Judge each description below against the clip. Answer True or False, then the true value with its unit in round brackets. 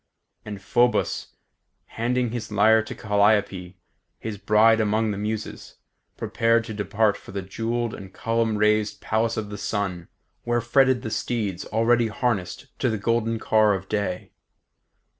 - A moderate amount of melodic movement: False (2.0 semitones)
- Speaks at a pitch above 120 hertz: False (110 Hz)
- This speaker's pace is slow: False (145 wpm)